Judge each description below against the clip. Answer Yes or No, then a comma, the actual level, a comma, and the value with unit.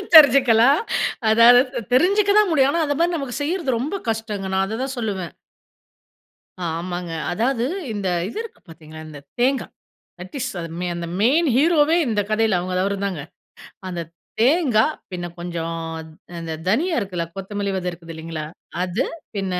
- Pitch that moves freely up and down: Yes, wide, 7.4 semitones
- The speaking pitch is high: Yes, high, 220 Hz